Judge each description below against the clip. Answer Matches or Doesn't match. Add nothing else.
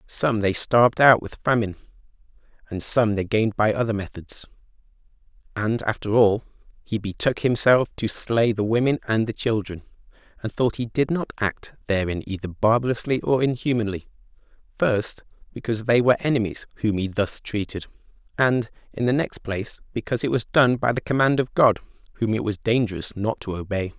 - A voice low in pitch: Matches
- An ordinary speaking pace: Matches